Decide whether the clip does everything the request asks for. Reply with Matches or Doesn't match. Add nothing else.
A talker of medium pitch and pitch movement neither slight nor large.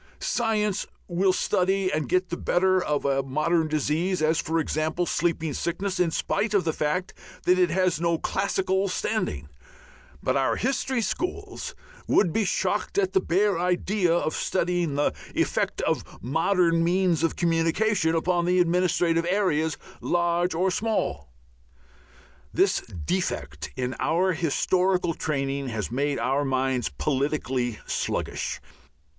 Matches